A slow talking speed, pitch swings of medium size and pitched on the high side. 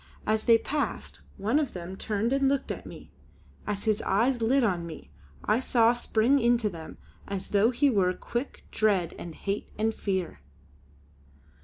No: average, 165 wpm; average, 3.7 semitones; high, 220 Hz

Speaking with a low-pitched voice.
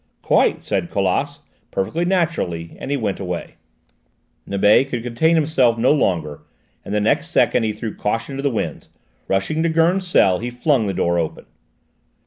Yes: low, 115 Hz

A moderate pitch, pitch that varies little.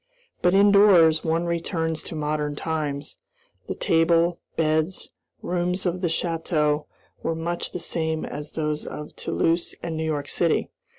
Yes: medium, 165 Hz; narrow, 1.9 semitones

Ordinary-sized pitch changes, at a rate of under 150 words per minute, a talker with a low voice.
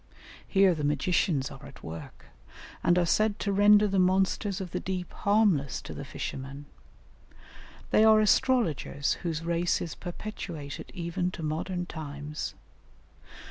No: average, 4.6 semitones; average, 140 wpm; medium, 175 Hz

